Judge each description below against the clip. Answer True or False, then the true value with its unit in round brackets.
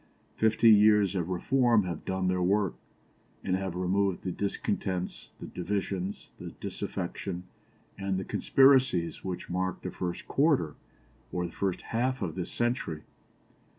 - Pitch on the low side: True (95 Hz)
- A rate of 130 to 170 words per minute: True (140 wpm)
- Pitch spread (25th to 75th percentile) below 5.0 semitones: True (2.8 semitones)